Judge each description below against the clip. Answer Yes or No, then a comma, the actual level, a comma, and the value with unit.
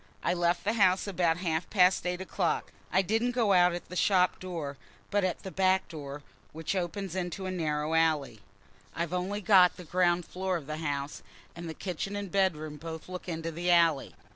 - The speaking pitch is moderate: Yes, medium, 175 Hz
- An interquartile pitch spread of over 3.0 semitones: No, narrow, 2.6 semitones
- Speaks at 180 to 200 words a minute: Yes, average, 195 wpm